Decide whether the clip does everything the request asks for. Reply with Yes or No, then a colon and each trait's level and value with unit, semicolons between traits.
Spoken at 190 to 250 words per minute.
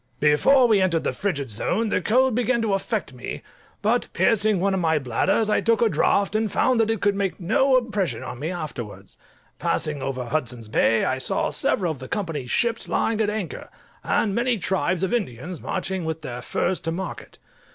Yes: average, 195 wpm